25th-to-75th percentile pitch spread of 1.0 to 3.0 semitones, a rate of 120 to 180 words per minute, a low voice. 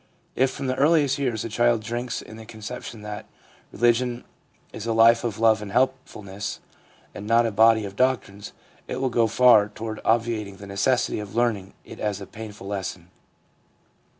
Yes: average, 2.7 semitones; average, 175 wpm; low, 115 Hz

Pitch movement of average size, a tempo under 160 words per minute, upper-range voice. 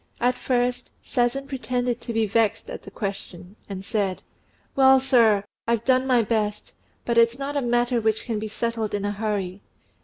No: average, 3.1 semitones; average, 180 wpm; high, 230 Hz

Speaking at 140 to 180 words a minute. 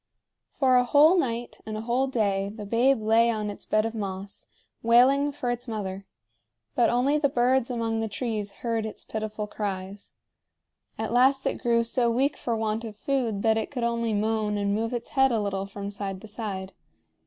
No: average, 195 wpm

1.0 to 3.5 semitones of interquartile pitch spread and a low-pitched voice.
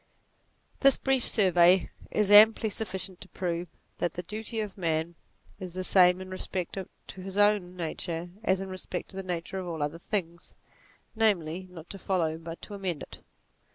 No: narrow, 2.5 semitones; medium, 185 Hz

